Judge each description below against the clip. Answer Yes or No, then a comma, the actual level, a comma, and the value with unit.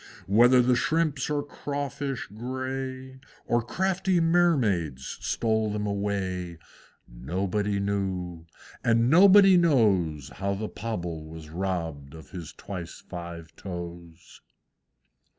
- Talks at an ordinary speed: No, slow, 105 wpm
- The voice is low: Yes, low, 100 Hz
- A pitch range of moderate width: No, wide, 7.2 semitones